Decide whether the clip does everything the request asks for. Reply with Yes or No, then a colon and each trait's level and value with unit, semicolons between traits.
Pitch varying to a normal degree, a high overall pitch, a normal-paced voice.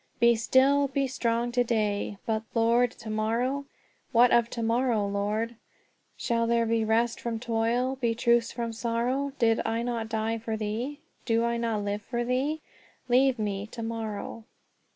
No: narrow, 1.6 semitones; high, 230 Hz; average, 165 wpm